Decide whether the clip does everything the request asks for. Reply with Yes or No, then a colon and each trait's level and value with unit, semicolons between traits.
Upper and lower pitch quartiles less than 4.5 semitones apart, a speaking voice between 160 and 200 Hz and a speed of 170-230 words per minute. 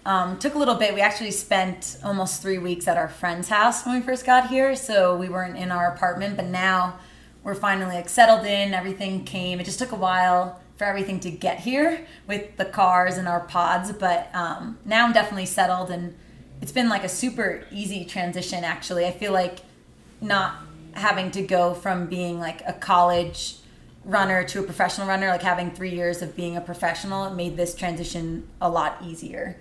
Yes: narrow, 2.4 semitones; medium, 185 Hz; average, 200 wpm